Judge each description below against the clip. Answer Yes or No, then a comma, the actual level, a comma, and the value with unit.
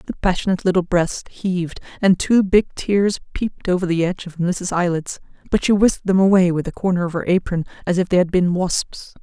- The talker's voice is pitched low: No, medium, 180 Hz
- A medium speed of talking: No, fast, 215 wpm